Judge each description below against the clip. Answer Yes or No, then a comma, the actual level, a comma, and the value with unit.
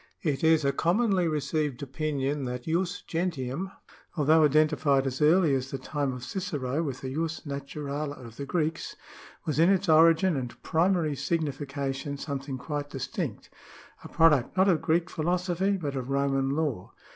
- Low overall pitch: No, medium, 150 Hz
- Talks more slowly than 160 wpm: No, average, 165 wpm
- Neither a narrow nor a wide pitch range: Yes, average, 3.3 semitones